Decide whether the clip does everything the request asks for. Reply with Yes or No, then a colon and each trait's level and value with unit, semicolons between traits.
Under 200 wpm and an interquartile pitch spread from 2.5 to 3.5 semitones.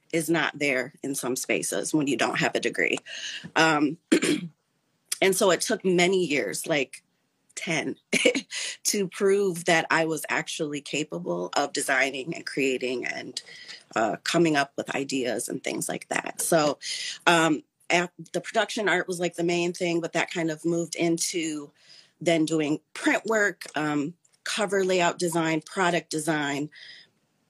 Yes: average, 150 wpm; average, 2.9 semitones